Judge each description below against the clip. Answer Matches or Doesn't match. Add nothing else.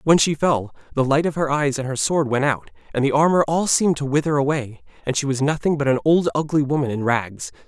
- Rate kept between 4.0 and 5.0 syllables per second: Doesn't match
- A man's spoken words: Matches